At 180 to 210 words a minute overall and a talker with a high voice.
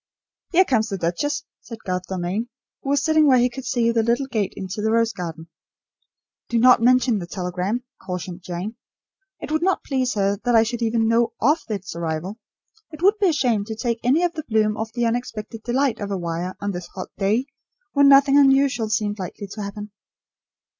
Yes: average, 200 wpm; high, 225 Hz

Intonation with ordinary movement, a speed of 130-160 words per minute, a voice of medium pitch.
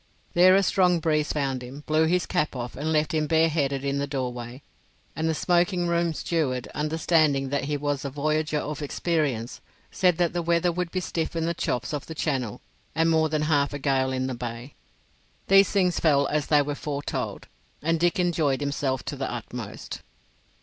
No: average, 3.2 semitones; average, 190 wpm; medium, 150 Hz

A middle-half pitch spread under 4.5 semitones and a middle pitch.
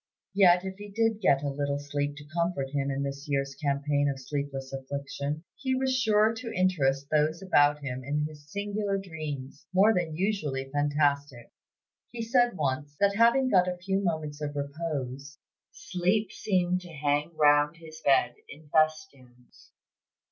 No: average, 4.8 semitones; medium, 150 Hz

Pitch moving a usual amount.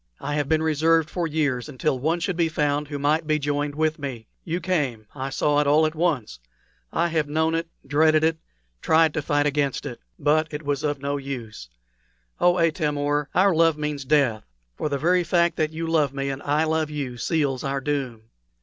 No: narrow, 2.2 semitones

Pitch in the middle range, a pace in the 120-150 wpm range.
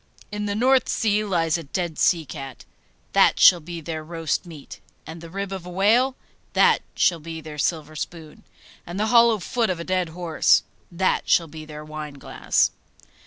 No: medium, 170 Hz; average, 180 wpm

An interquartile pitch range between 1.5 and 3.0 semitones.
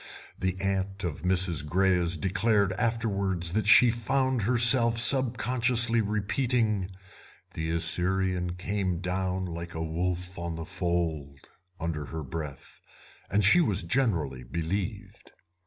No: average, 4.5 semitones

